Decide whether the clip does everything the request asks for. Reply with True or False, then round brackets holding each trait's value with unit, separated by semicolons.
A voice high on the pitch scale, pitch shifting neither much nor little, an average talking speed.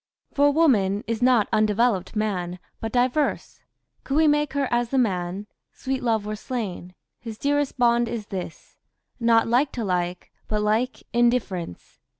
True (230 Hz; 3.9 semitones; 160 wpm)